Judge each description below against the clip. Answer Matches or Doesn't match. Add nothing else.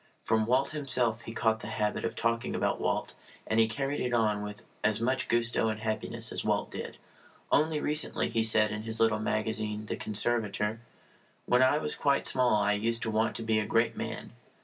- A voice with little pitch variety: Matches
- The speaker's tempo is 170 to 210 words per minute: Matches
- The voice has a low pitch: Matches